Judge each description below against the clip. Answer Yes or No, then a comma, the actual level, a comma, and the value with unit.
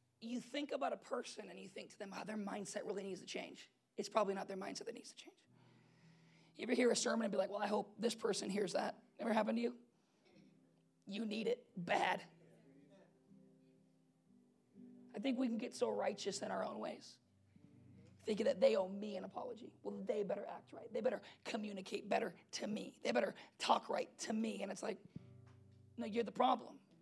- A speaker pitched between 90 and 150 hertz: No, high, 210 Hz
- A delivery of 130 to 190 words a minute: No, fast, 205 wpm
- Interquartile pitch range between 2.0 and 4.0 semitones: Yes, average, 3.6 semitones